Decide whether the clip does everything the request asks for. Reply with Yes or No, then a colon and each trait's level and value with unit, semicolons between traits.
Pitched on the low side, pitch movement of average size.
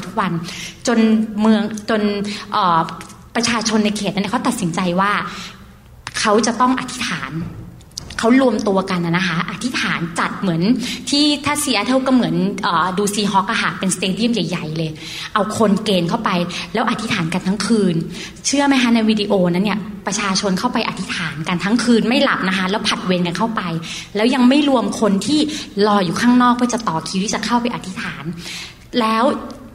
No: high, 210 Hz; average, 4.2 semitones